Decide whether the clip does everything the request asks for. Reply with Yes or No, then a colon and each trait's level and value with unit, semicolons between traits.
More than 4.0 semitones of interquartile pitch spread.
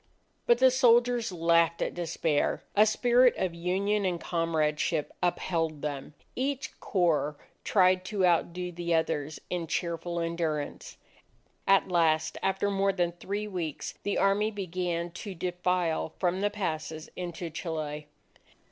No: average, 3.2 semitones